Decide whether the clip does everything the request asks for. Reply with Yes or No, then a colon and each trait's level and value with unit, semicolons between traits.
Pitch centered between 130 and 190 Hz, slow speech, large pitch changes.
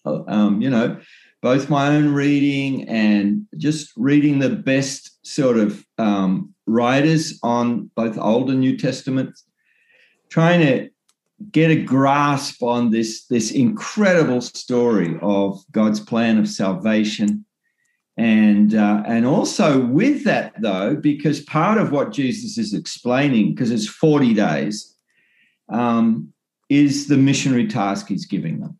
Yes: medium, 140 Hz; slow, 130 wpm; wide, 6.2 semitones